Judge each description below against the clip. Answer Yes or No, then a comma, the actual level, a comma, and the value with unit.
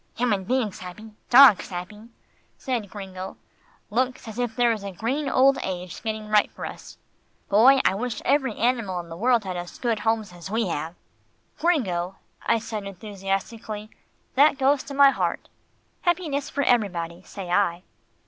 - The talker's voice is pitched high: Yes, high, 215 Hz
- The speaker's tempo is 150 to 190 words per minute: Yes, average, 160 wpm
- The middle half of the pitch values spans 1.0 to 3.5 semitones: No, average, 4.9 semitones